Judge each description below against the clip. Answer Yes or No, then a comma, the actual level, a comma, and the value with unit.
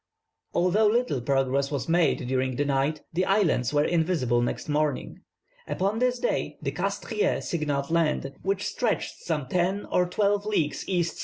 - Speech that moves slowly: No, average, 155 wpm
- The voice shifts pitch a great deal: Yes, wide, 5.8 semitones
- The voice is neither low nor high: Yes, medium, 165 Hz